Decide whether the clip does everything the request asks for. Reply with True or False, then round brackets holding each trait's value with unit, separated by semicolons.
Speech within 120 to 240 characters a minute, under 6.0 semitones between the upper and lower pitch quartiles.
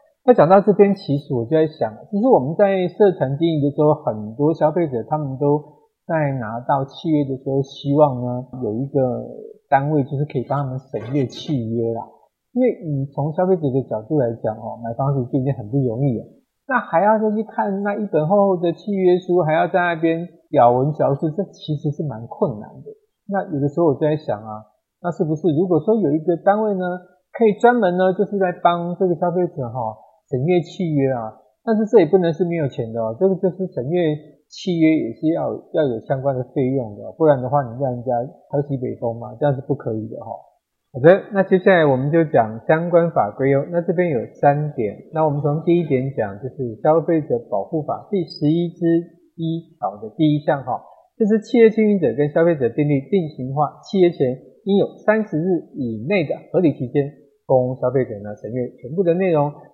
False (305 characters per minute; 5.1 semitones)